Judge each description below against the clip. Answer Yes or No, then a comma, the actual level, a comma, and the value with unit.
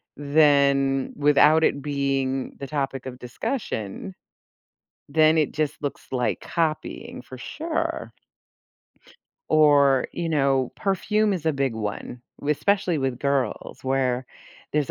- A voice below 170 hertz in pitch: Yes, medium, 140 Hz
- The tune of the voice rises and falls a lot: No, narrow, 2.6 semitones